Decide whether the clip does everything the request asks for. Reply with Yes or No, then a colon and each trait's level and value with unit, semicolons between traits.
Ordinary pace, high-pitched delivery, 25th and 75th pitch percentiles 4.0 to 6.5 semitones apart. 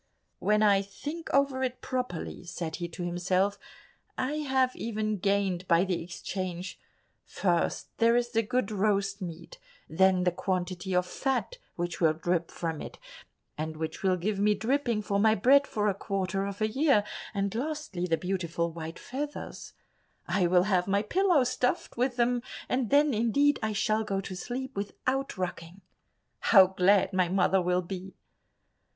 Yes: average, 165 wpm; high, 200 Hz; average, 5.1 semitones